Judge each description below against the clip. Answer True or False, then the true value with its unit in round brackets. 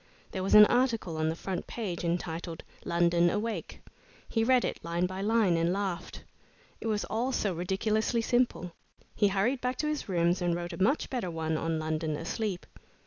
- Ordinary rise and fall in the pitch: True (4.7 semitones)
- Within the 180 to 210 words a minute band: True (185 wpm)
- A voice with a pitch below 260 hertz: True (190 Hz)